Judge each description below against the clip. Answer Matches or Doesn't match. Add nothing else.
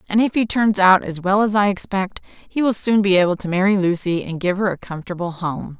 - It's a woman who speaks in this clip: Matches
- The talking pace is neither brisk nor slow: Doesn't match